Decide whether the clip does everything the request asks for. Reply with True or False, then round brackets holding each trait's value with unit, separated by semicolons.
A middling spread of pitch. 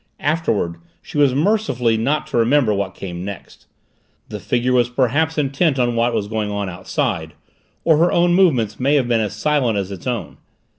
False (5.9 semitones)